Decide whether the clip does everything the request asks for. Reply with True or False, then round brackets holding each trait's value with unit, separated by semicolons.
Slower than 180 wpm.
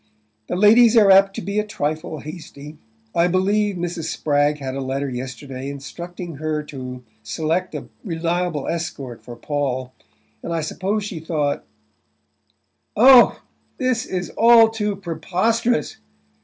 True (140 wpm)